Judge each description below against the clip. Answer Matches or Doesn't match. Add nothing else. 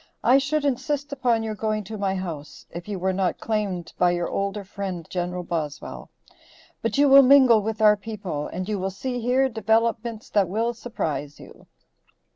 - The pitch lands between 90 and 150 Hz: Doesn't match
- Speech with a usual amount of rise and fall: Matches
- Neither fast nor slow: Matches